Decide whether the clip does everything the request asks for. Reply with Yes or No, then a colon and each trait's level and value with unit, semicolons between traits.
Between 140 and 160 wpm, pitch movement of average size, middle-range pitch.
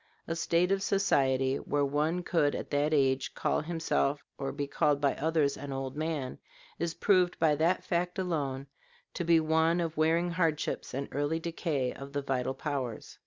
No: average, 175 wpm; average, 3.3 semitones; medium, 150 Hz